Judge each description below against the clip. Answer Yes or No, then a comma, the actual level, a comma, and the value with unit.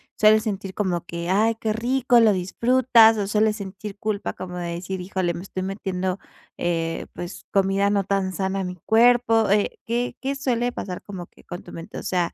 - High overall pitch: Yes, high, 195 Hz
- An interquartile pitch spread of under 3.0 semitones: No, average, 3.4 semitones